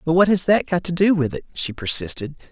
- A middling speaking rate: No, fast, 260 wpm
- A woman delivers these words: No, male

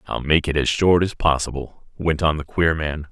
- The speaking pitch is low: Yes, very low, 80 Hz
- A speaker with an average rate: No, fast, 230 wpm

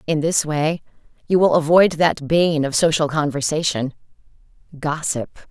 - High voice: No, medium, 155 Hz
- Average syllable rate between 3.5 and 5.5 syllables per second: Yes, 4.6 syllables/s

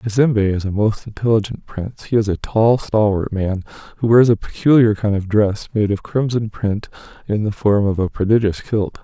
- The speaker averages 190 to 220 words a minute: Yes, average, 200 wpm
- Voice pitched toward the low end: Yes, low, 105 Hz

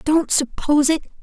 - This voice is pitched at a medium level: No, very high, 300 Hz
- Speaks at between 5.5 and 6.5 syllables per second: No, 5.1 syllables/s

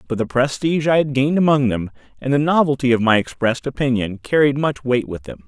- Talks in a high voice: No, low, 130 Hz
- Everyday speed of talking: No, fast, 220 wpm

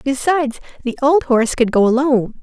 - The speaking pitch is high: Yes, very high, 260 Hz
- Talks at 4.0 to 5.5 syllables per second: No, 6.1 syllables/s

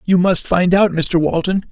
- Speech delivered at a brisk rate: Yes, fast, 210 wpm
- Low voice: No, medium, 180 Hz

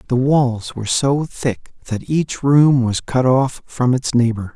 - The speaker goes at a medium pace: Yes, average, 185 wpm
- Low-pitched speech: Yes, low, 125 Hz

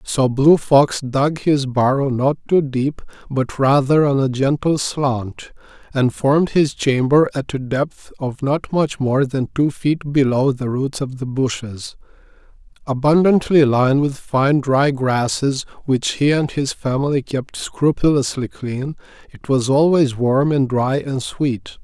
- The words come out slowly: No, average, 155 wpm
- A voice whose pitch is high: No, low, 135 Hz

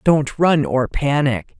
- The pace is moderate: Yes, average, 150 wpm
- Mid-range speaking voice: Yes, medium, 150 Hz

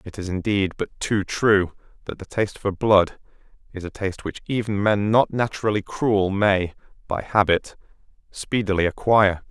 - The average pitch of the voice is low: Yes, low, 100 Hz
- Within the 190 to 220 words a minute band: No, average, 160 wpm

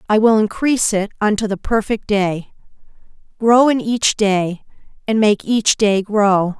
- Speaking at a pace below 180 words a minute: Yes, average, 155 wpm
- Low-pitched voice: No, high, 210 Hz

